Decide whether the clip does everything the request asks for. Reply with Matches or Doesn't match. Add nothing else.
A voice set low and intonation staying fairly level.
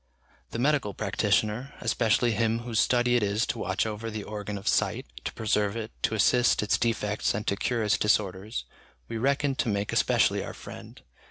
Matches